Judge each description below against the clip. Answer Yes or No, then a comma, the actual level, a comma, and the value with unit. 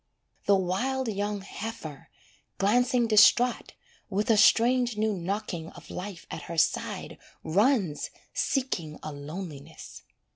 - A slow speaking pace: Yes, slow, 115 wpm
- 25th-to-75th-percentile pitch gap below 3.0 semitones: No, average, 5.3 semitones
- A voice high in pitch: Yes, high, 205 Hz